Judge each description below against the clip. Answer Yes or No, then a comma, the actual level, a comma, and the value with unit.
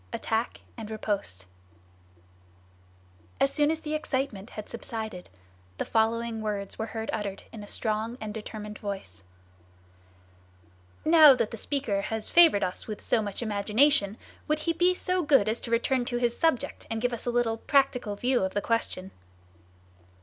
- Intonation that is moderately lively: Yes, average, 3.9 semitones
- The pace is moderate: Yes, average, 160 wpm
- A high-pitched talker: Yes, high, 225 Hz